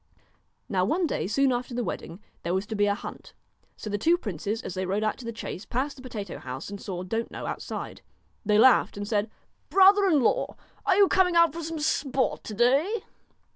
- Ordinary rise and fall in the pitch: No, wide, 7.5 semitones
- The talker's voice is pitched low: No, high, 235 Hz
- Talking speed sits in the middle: No, fast, 215 wpm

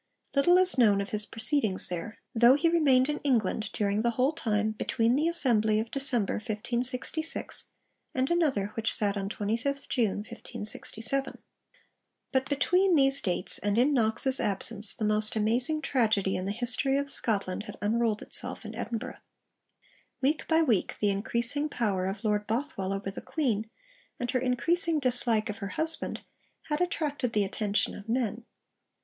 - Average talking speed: Yes, average, 160 wpm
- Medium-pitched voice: No, high, 235 Hz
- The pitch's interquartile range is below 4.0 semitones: No, average, 4.6 semitones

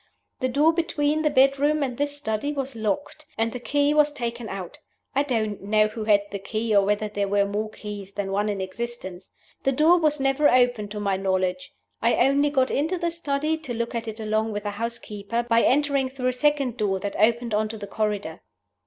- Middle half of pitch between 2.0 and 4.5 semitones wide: No, average, 5.2 semitones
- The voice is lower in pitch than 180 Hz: No, high, 235 Hz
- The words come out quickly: Yes, fast, 215 wpm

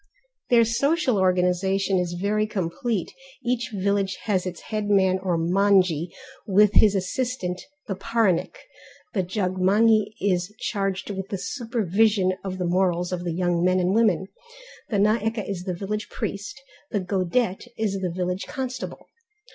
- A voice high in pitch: Yes, high, 195 Hz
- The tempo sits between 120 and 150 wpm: Yes, average, 140 wpm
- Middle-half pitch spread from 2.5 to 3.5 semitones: Yes, average, 2.8 semitones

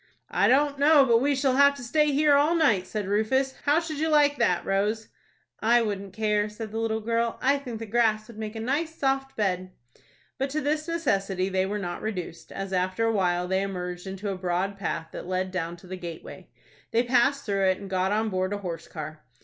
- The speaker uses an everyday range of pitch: No, wide, 6.2 semitones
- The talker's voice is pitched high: Yes, high, 215 Hz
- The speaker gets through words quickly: Yes, fast, 220 wpm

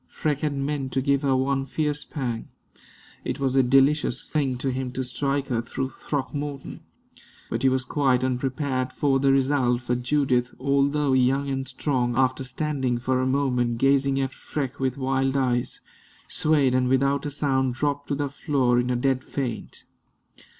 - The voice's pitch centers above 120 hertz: Yes, low, 135 Hz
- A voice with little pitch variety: Yes, narrow, 1.6 semitones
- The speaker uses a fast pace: No, average, 170 wpm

